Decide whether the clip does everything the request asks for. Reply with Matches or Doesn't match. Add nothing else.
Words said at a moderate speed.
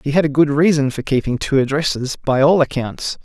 Doesn't match